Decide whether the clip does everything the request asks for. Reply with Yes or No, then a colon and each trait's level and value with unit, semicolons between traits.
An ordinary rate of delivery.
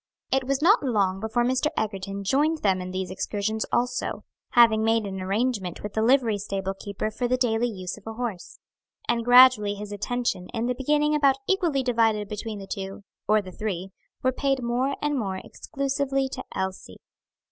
Yes: average, 180 wpm